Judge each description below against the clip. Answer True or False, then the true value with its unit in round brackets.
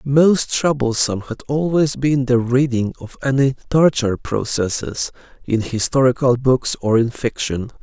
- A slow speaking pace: True (130 wpm)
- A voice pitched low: True (125 Hz)